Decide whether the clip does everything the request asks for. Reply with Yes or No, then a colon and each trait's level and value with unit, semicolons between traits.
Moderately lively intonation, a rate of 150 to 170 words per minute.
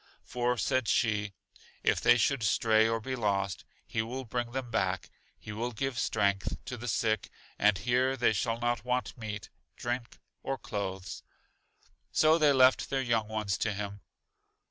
Yes: average, 3.1 semitones; average, 165 wpm